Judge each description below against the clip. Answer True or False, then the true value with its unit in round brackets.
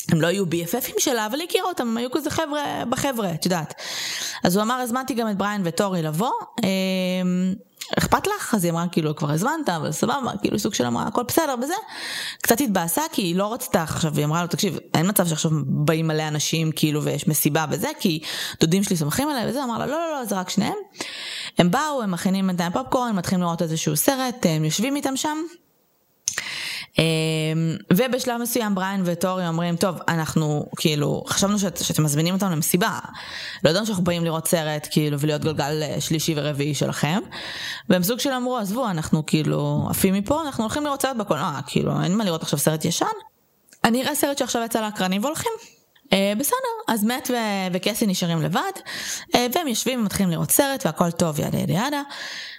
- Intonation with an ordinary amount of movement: False (7.3 semitones)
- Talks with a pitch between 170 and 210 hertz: True (190 Hz)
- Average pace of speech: False (185 wpm)